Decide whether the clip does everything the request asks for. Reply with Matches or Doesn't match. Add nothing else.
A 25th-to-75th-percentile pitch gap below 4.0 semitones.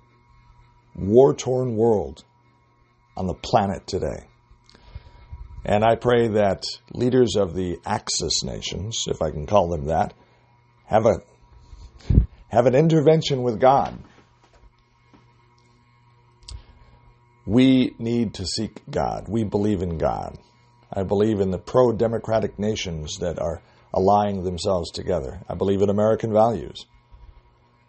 Matches